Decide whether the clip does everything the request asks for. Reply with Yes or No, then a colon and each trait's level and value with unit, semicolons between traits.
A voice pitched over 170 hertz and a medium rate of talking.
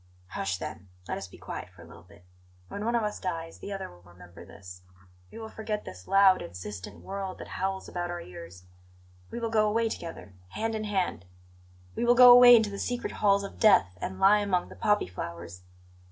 No: medium, 185 Hz; fast, 210 wpm